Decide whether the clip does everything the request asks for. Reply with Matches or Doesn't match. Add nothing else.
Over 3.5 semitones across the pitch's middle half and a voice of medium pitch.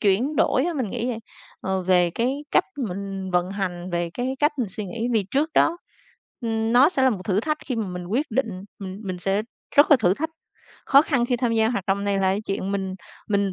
Doesn't match